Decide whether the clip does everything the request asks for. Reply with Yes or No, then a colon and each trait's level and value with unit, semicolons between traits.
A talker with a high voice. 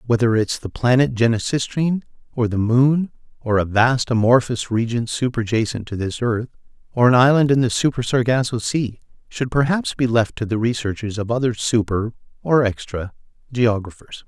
No: low, 120 Hz